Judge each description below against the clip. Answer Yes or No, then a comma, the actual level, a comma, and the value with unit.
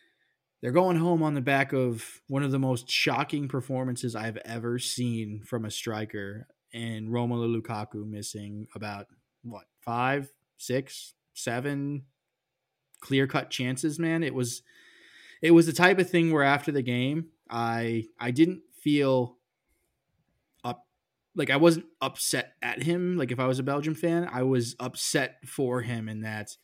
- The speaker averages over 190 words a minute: No, average, 155 wpm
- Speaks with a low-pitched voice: Yes, low, 130 Hz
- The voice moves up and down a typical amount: Yes, average, 4.0 semitones